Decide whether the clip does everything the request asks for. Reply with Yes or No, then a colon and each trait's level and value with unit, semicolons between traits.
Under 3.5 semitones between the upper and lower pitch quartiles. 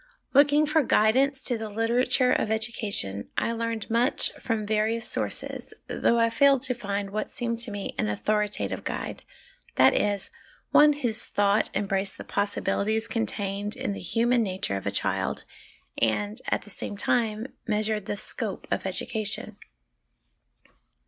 Yes: average, 2.7 semitones